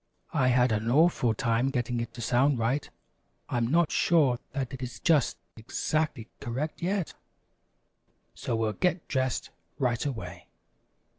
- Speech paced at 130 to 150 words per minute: Yes, average, 140 wpm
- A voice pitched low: Yes, low, 130 Hz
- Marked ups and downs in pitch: No, average, 3.8 semitones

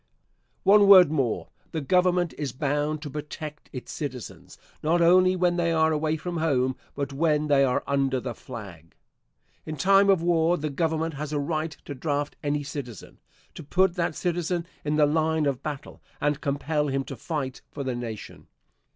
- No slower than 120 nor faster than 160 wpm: No, average, 175 wpm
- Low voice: No, medium, 150 Hz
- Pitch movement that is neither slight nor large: Yes, average, 3.1 semitones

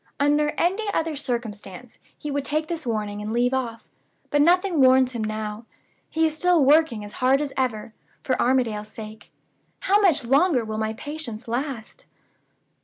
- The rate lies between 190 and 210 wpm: No, average, 165 wpm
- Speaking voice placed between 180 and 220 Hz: No, very high, 260 Hz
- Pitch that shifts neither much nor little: No, wide, 5.7 semitones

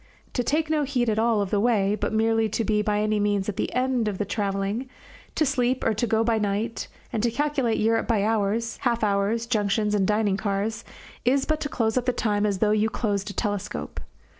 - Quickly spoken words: Yes, fast, 220 wpm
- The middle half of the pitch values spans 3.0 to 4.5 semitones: No, narrow, 2.4 semitones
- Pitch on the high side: Yes, high, 220 Hz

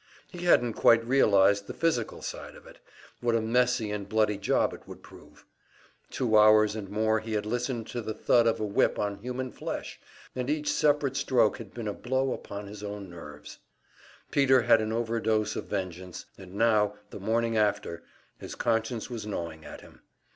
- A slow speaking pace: No, average, 185 wpm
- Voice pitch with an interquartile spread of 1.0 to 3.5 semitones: Yes, average, 2.9 semitones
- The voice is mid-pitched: No, low, 110 Hz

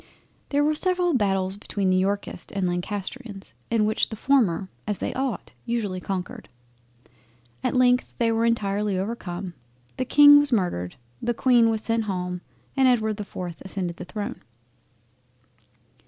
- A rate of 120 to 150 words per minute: Yes, average, 140 wpm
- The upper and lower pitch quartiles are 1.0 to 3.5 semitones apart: No, average, 4.4 semitones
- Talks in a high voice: Yes, high, 210 Hz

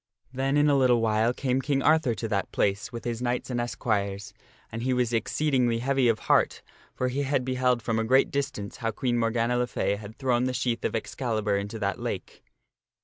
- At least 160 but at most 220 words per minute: Yes, fast, 205 wpm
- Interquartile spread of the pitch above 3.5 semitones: No, narrow, 2.5 semitones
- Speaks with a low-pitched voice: Yes, low, 120 Hz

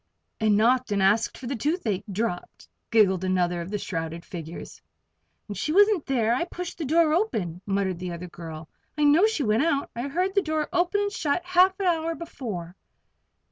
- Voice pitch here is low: No, high, 240 Hz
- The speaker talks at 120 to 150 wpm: No, average, 185 wpm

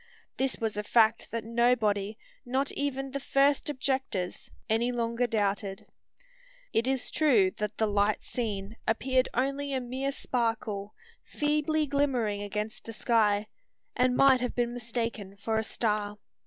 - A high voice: Yes, high, 235 Hz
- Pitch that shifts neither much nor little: Yes, average, 3.9 semitones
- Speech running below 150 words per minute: Yes, average, 140 wpm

